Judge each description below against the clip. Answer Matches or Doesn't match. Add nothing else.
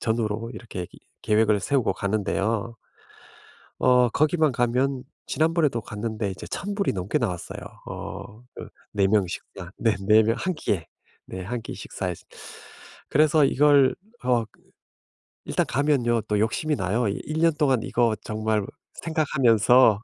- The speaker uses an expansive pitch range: Doesn't match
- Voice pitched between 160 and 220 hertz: Doesn't match